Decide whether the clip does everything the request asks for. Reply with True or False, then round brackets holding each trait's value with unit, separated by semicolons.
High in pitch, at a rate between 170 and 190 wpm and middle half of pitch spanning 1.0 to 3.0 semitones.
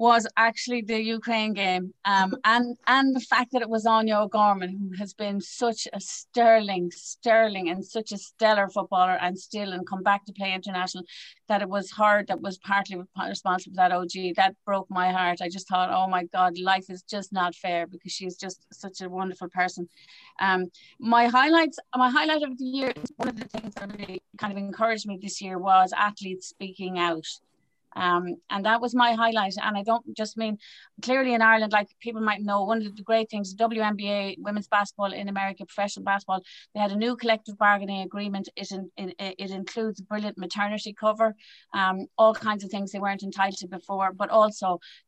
False (200 Hz; 200 wpm; 2.7 semitones)